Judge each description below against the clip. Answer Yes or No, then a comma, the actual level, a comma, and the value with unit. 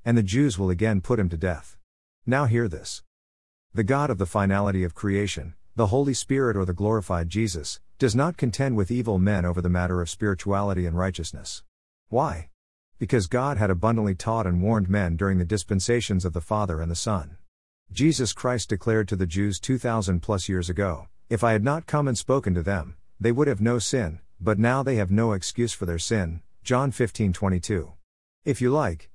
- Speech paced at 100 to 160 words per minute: No, average, 195 wpm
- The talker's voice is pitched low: Yes, low, 100 Hz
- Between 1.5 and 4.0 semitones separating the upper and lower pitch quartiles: No, average, 4.7 semitones